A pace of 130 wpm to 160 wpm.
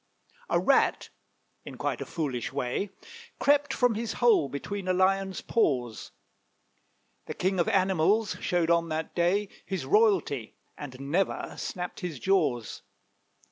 Yes: slow, 135 wpm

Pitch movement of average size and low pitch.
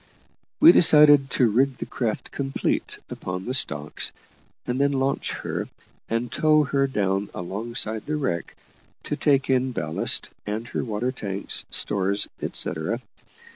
Yes: average, 5.0 semitones; low, 125 Hz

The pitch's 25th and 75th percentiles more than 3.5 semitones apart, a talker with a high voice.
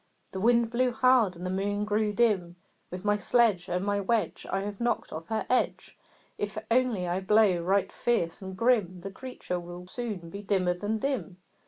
Yes: average, 4.1 semitones; high, 205 Hz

